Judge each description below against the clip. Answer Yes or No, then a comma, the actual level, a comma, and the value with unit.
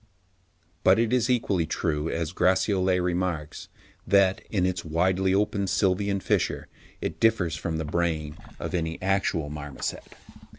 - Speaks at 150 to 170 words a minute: No, slow, 135 wpm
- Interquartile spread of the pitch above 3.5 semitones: No, average, 3.2 semitones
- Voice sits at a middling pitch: No, very low, 90 Hz